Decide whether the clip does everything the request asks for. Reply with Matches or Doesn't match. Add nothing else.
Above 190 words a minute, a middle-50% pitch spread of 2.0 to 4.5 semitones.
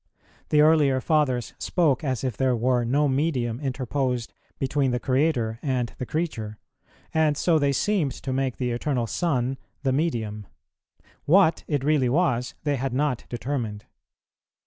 Doesn't match